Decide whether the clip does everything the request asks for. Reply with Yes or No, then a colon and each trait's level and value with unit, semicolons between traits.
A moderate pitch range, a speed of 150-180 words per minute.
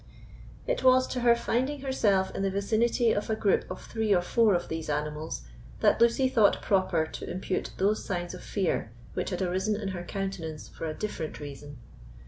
No: average, 4.2 semitones; average, 190 wpm